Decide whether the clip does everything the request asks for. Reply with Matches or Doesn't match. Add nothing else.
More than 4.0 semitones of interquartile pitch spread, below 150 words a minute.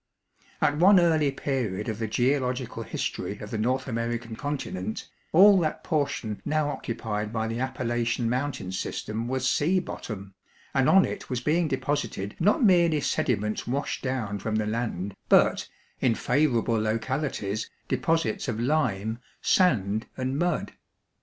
Matches